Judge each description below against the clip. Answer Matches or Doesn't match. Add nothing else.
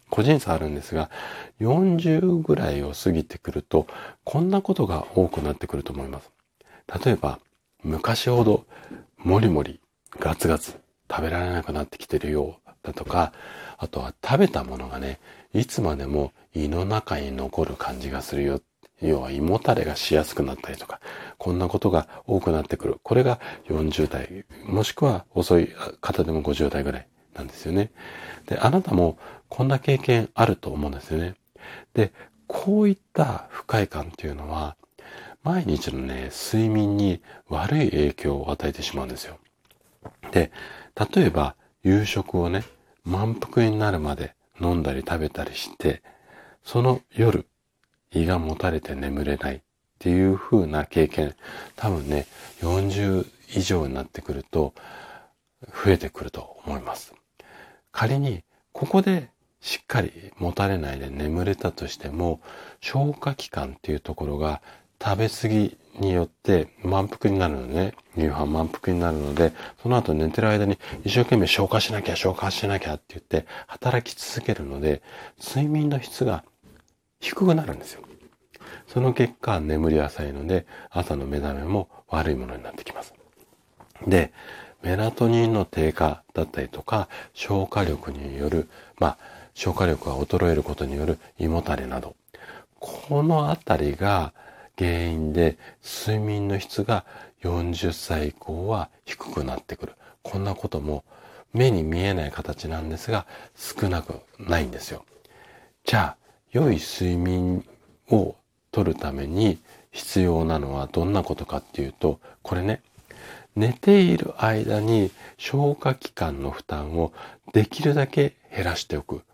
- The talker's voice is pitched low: Matches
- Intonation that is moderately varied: Doesn't match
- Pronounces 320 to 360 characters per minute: Doesn't match